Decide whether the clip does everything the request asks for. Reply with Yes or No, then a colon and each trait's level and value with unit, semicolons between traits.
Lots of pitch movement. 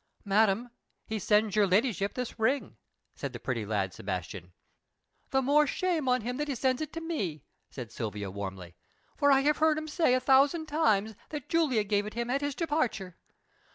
Yes: wide, 7.9 semitones